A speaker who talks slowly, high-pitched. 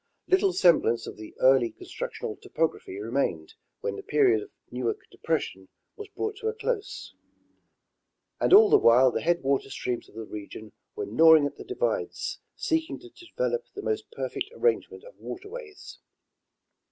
No: average, 150 wpm; very high, 315 Hz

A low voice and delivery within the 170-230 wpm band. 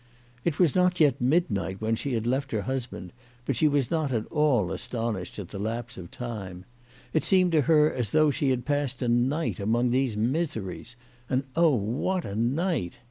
Yes: low, 125 Hz; average, 190 wpm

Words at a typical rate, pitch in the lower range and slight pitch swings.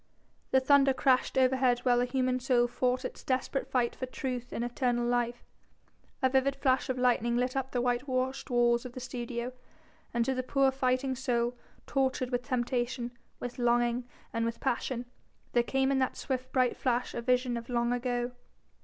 No: average, 180 wpm; very high, 250 Hz; narrow, 1.3 semitones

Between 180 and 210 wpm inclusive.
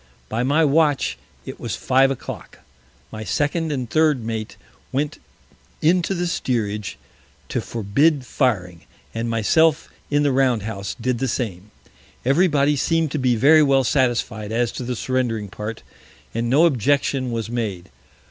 No: average, 155 wpm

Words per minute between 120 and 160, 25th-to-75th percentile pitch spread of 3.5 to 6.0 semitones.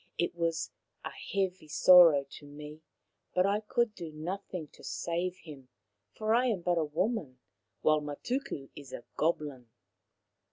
Yes: average, 150 wpm; average, 4.2 semitones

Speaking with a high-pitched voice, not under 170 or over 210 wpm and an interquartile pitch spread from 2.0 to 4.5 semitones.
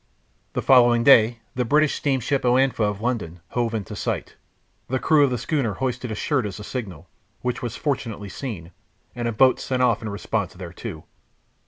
No: low, 120 Hz; average, 180 wpm; average, 3.6 semitones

